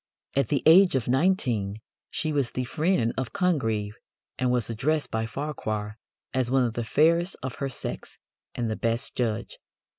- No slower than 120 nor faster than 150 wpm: No, average, 170 wpm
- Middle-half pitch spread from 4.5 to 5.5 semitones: Yes, average, 4.9 semitones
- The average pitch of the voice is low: Yes, low, 130 Hz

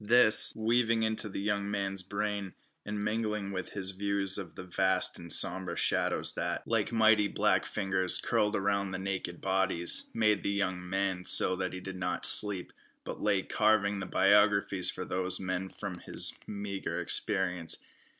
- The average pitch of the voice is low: Yes, low, 100 Hz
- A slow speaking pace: No, average, 165 wpm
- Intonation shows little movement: Yes, narrow, 2.0 semitones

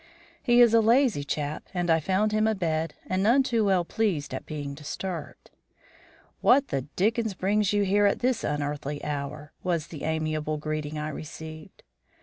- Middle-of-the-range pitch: Yes, medium, 170 Hz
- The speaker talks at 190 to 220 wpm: No, average, 165 wpm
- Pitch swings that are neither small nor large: No, wide, 5.9 semitones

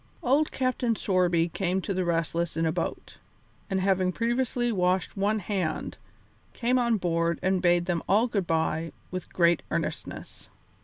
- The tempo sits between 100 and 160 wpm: Yes, average, 155 wpm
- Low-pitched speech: No, medium, 185 Hz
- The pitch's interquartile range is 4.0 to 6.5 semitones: Yes, average, 4.3 semitones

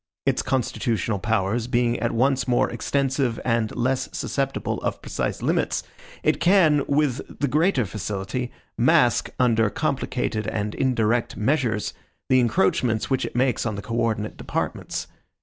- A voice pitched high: No, low, 120 Hz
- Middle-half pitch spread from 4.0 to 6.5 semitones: No, average, 3.4 semitones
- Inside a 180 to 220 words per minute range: No, average, 140 wpm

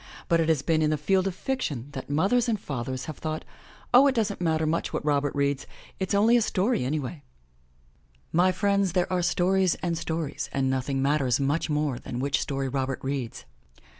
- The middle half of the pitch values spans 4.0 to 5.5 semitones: Yes, average, 5.2 semitones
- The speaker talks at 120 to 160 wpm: No, average, 195 wpm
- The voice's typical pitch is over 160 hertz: No, medium, 155 Hz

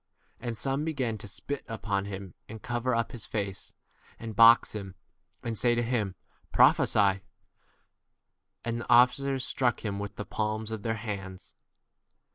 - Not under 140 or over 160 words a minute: Yes, average, 150 wpm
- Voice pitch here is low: Yes, low, 115 Hz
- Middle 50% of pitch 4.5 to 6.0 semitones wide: No, average, 3.1 semitones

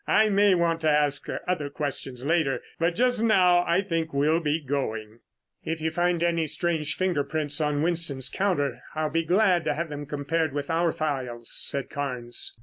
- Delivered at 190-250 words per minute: No, average, 180 wpm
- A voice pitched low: No, medium, 155 Hz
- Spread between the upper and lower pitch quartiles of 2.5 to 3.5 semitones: Yes, average, 3.2 semitones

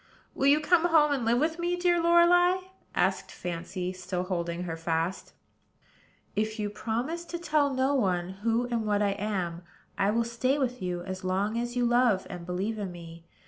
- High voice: Yes, high, 220 Hz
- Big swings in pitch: Yes, wide, 7.4 semitones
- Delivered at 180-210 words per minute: Yes, average, 190 wpm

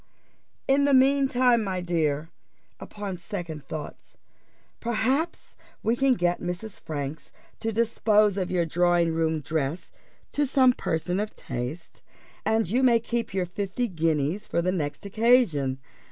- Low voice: No, medium, 185 Hz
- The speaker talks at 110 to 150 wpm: Yes, average, 140 wpm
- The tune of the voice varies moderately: No, wide, 6.2 semitones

